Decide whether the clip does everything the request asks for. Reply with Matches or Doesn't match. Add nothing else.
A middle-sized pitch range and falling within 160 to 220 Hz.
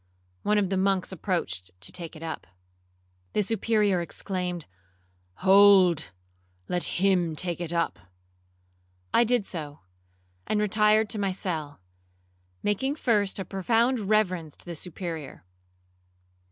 Matches